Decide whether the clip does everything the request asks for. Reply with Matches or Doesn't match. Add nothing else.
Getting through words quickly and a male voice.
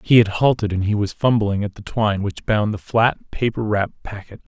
Matches